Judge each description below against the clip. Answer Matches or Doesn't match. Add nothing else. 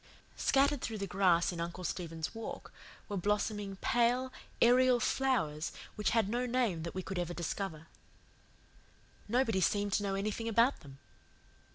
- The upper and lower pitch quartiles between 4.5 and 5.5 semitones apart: Matches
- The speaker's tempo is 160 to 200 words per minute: Doesn't match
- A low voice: Doesn't match